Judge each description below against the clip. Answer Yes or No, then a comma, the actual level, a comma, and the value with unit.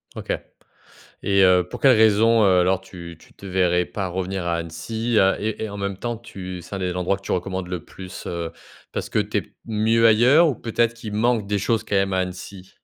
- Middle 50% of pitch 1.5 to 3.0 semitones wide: No, average, 3.4 semitones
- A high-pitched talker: No, low, 100 Hz